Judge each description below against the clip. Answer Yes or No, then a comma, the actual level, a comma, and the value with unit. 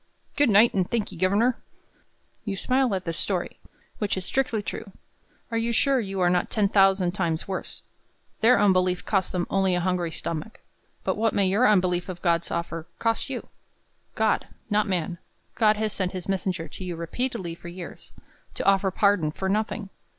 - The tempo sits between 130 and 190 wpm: Yes, average, 180 wpm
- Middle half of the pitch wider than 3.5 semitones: No, average, 3.2 semitones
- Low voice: No, high, 195 Hz